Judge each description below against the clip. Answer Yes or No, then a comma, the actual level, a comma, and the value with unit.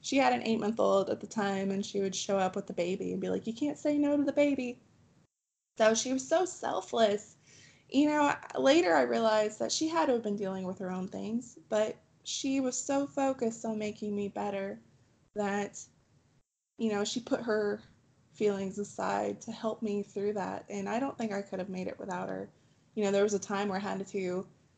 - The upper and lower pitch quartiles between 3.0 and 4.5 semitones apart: Yes, average, 4.0 semitones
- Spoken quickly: Yes, fast, 220 wpm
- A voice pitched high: Yes, high, 210 Hz